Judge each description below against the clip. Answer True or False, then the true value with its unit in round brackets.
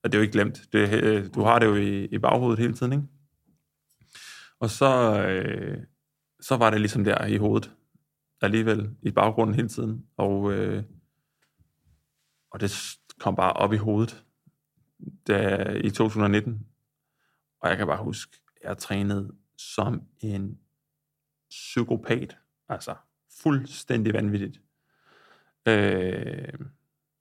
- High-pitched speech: False (110 Hz)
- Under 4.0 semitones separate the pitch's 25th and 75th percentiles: False (4.9 semitones)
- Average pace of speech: False (125 wpm)